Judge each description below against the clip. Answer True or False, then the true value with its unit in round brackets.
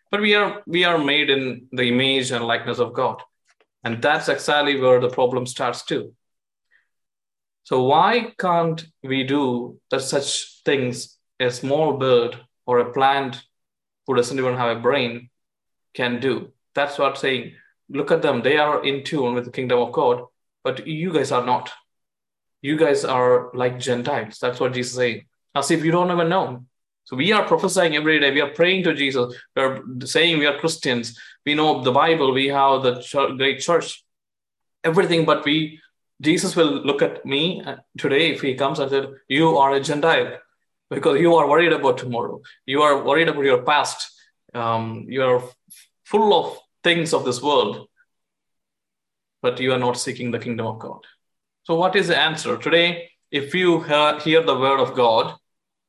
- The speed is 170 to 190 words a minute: True (180 wpm)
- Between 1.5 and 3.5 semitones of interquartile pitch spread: False (4.7 semitones)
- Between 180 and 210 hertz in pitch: False (140 Hz)